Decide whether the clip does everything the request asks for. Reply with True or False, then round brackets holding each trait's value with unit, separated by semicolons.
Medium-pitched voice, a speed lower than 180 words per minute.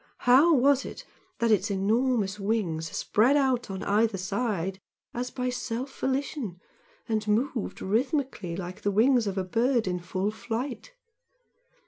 False (225 Hz; 140 wpm)